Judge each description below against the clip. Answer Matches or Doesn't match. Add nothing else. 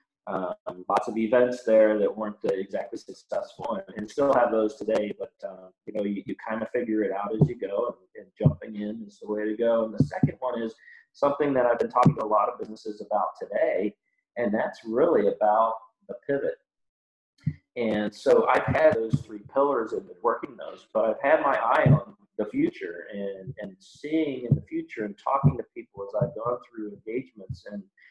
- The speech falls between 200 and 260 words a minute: Matches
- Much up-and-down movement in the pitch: Matches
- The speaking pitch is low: Matches